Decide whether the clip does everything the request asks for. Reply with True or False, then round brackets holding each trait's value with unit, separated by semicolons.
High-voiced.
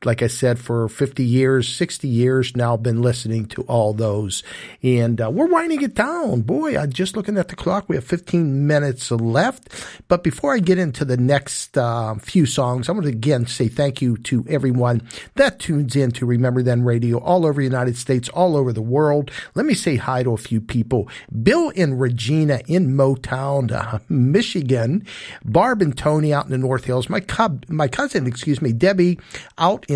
False (135 Hz)